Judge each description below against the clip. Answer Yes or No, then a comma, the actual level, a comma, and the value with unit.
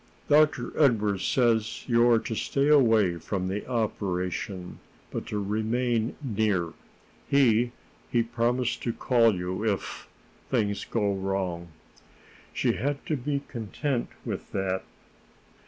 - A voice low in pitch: Yes, low, 110 Hz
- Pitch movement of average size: Yes, average, 3.9 semitones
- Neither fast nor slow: No, slow, 120 wpm